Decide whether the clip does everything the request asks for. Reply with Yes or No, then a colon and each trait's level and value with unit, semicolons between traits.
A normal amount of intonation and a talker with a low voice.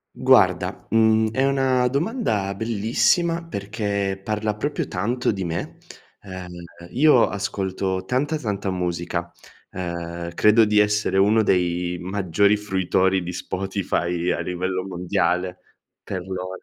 Yes: average, 3.4 semitones; low, 100 Hz